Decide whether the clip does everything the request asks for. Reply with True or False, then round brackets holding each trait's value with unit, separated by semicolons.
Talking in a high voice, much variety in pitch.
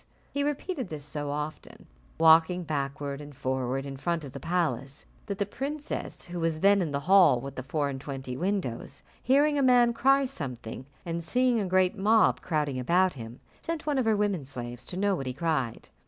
False (165 Hz; 6.8 semitones)